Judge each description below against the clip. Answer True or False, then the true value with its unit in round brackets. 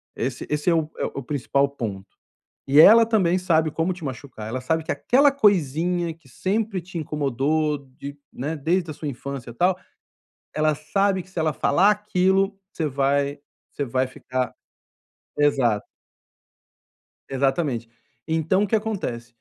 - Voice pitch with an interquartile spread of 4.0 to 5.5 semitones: True (5.1 semitones)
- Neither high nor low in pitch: True (155 Hz)